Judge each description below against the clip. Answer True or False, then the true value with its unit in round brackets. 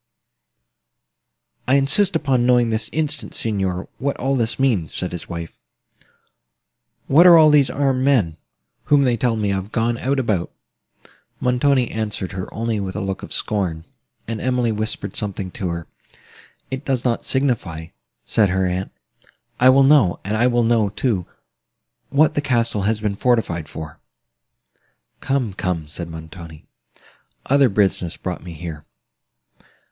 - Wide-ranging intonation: True (6.0 semitones)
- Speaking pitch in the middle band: False (110 Hz)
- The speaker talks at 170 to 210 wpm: False (145 wpm)